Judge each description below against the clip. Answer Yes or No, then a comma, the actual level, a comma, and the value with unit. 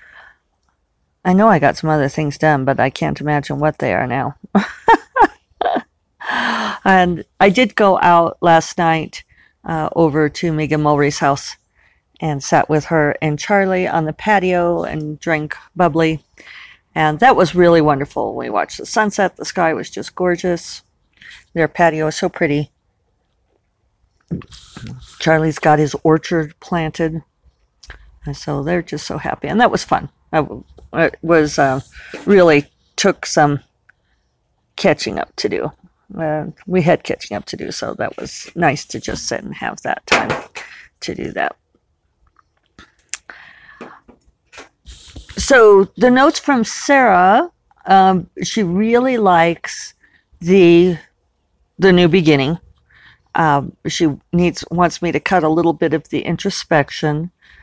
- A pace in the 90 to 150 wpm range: Yes, average, 140 wpm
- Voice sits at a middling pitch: Yes, medium, 165 Hz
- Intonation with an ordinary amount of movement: Yes, average, 3.6 semitones